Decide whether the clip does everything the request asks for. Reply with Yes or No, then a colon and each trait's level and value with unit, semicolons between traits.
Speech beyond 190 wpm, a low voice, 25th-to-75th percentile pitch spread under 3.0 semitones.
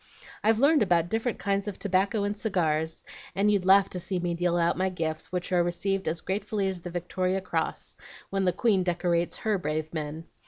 No: average, 200 wpm; medium, 185 Hz; narrow, 2.6 semitones